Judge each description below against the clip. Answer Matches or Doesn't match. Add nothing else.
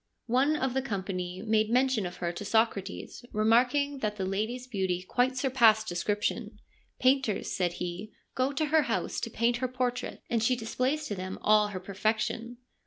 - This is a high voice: Matches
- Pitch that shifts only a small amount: Doesn't match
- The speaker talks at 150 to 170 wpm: Doesn't match